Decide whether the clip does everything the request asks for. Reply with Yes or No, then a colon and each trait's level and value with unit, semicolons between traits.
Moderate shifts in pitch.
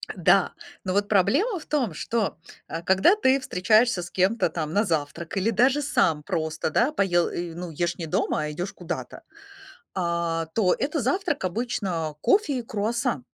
No: wide, 6.2 semitones